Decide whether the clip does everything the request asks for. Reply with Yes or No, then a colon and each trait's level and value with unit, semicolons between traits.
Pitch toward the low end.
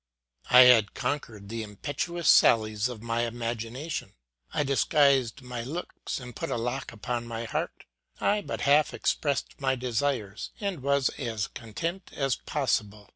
Yes: low, 125 Hz